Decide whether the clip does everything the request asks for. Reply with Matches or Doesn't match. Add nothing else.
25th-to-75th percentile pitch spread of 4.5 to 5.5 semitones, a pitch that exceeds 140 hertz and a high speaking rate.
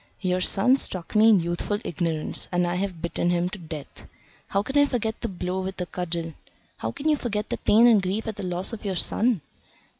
Doesn't match